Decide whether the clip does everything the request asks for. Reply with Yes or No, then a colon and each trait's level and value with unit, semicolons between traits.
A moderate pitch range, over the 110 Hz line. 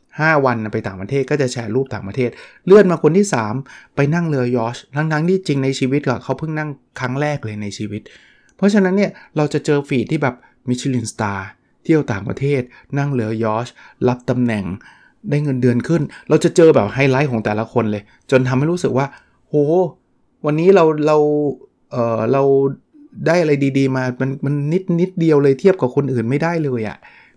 Yes: average, 3.7 semitones; low, 135 Hz